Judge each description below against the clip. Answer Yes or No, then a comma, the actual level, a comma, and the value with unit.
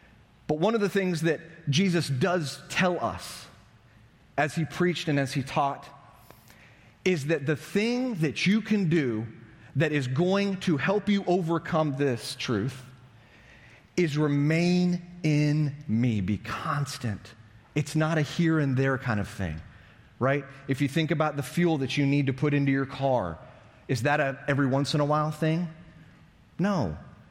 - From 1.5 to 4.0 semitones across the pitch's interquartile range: No, average, 4.5 semitones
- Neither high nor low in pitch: Yes, medium, 145 Hz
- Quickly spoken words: No, average, 165 wpm